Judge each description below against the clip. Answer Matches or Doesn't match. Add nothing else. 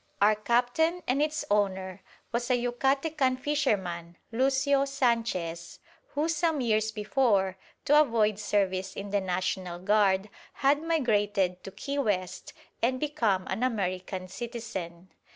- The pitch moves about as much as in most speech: Doesn't match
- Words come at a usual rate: Doesn't match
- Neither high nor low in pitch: Doesn't match